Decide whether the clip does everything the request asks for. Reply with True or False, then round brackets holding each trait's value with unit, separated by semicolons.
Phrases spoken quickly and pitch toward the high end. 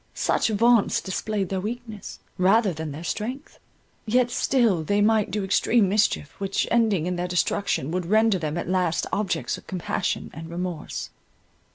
False (155 wpm; 195 Hz)